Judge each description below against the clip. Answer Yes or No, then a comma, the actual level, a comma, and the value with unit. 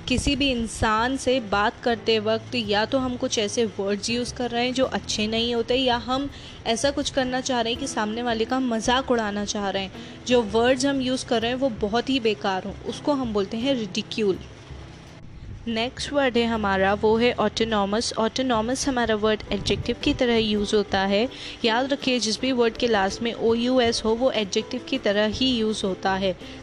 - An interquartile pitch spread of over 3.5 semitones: No, average, 2.9 semitones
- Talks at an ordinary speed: No, fast, 205 wpm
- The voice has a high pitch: Yes, high, 230 Hz